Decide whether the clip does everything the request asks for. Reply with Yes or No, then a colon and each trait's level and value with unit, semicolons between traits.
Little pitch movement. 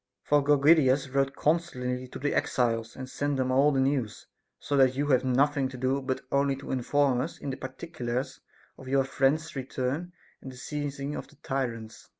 Yes: narrow, 1.9 semitones